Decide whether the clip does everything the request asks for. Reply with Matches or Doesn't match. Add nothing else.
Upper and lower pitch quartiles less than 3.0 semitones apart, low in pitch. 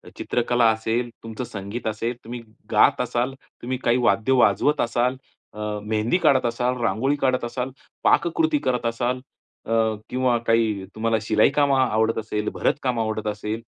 Matches